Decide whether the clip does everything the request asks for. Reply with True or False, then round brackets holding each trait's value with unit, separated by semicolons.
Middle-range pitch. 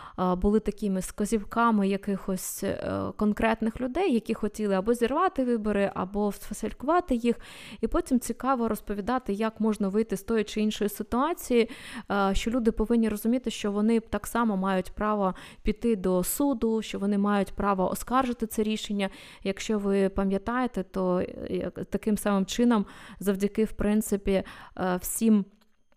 False (215 Hz)